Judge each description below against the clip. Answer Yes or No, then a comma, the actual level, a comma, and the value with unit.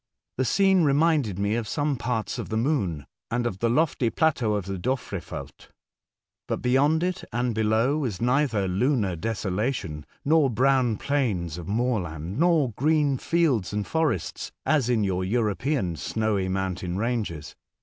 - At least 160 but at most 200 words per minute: No, average, 150 wpm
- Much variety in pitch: Yes, wide, 6.2 semitones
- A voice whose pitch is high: No, low, 115 Hz